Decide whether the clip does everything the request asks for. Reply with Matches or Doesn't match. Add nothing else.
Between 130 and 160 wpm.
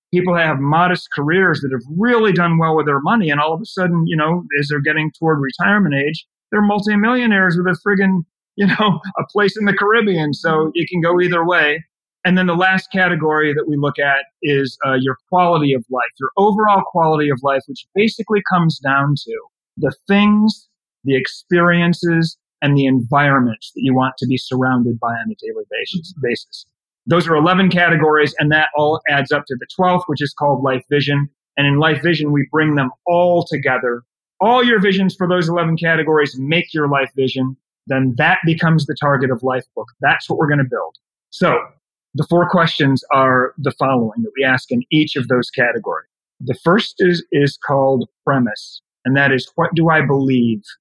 Doesn't match